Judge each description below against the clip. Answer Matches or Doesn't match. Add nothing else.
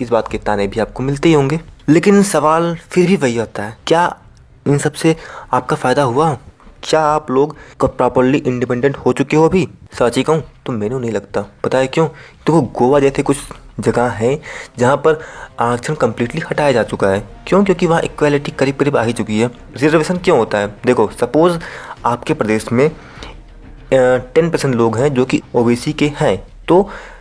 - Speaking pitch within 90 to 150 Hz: Matches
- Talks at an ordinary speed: Doesn't match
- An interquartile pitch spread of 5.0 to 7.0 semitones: Doesn't match